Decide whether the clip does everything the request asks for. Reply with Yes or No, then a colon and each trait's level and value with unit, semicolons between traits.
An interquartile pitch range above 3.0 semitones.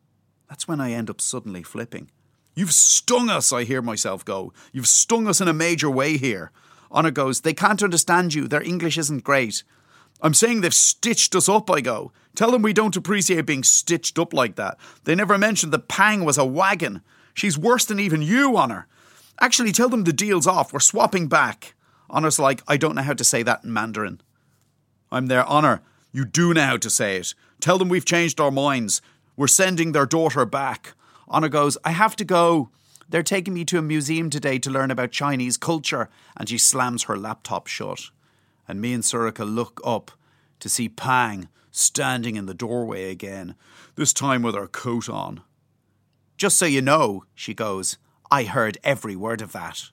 Yes: wide, 5.6 semitones